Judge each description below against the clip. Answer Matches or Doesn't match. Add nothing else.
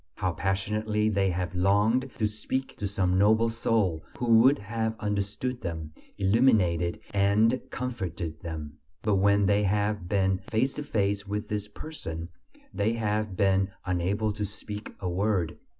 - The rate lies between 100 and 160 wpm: Matches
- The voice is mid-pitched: Doesn't match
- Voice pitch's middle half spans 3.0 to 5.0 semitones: Doesn't match